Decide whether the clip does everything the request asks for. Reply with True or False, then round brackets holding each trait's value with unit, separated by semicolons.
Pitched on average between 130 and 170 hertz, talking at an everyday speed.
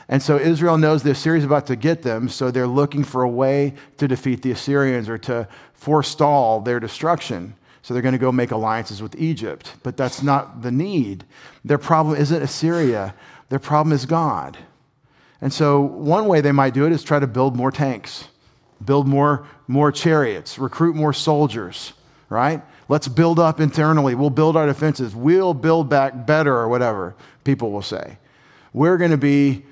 True (140 Hz; 185 wpm)